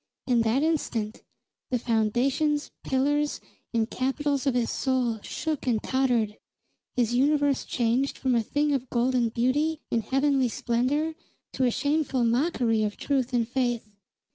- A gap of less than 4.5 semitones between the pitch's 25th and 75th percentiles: Yes, average, 3.3 semitones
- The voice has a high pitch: Yes, very high, 255 Hz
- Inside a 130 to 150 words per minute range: Yes, average, 140 wpm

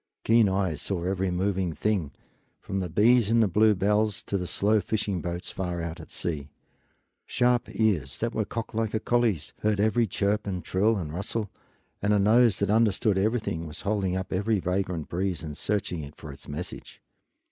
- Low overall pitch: Yes, low, 100 Hz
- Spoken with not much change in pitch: No, average, 3.6 semitones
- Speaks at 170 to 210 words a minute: Yes, average, 185 wpm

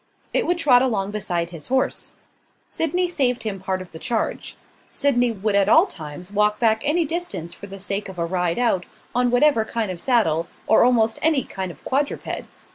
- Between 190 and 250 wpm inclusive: Yes, average, 195 wpm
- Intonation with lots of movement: Yes, wide, 5.8 semitones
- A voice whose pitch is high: Yes, high, 220 Hz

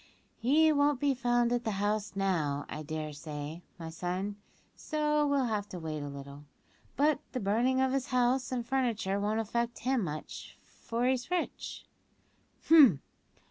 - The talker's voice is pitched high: Yes, high, 230 Hz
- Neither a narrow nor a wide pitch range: No, wide, 6.8 semitones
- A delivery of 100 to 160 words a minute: Yes, average, 155 wpm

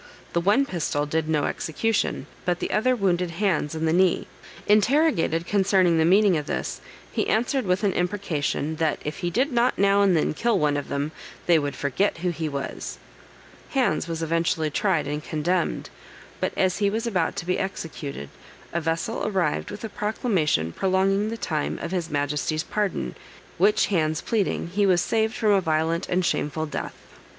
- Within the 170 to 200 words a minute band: Yes, average, 180 wpm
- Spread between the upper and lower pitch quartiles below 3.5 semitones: No, average, 4.3 semitones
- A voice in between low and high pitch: Yes, medium, 175 Hz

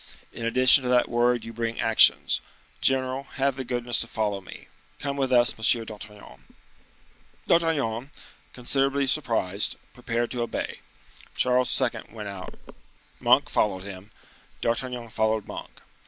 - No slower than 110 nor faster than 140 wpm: Yes, slow, 135 wpm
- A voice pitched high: No, low, 120 Hz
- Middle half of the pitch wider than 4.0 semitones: No, average, 2.8 semitones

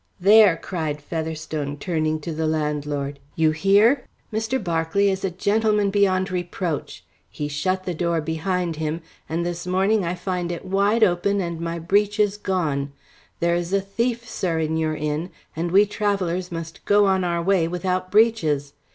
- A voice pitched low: No, medium, 175 Hz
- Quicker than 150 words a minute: Yes, average, 165 wpm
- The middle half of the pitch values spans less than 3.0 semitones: No, average, 3.6 semitones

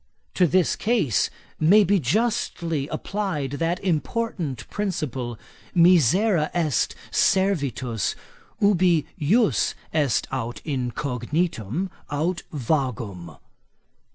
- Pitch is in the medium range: Yes, medium, 160 Hz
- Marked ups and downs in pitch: Yes, wide, 6.4 semitones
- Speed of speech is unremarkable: No, slow, 85 wpm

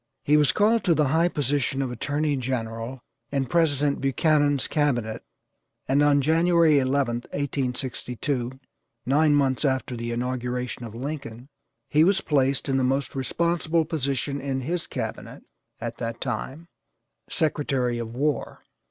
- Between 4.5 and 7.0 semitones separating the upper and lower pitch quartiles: No, average, 3.2 semitones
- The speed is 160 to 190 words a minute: No, slow, 135 wpm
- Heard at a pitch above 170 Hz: No, low, 135 Hz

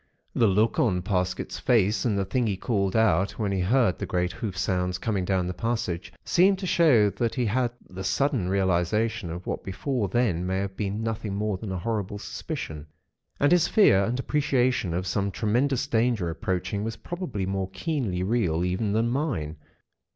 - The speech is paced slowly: No, average, 185 wpm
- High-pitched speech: No, low, 100 Hz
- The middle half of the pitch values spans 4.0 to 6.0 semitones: Yes, average, 4.4 semitones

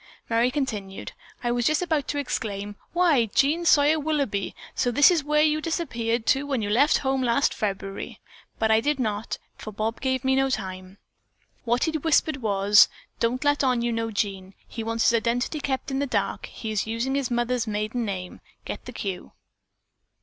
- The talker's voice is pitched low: No, high, 240 Hz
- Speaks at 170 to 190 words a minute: Yes, average, 185 wpm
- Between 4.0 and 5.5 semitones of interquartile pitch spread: Yes, average, 4.7 semitones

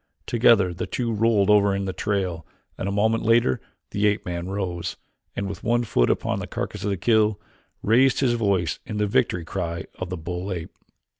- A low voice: Yes, low, 100 Hz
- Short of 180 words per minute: No, average, 200 wpm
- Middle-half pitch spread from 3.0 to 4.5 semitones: Yes, average, 3.5 semitones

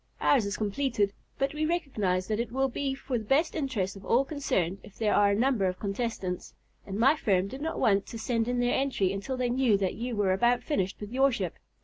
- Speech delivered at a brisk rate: Yes, fast, 235 wpm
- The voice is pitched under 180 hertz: No, high, 230 Hz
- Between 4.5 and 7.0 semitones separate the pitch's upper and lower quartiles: Yes, average, 5.2 semitones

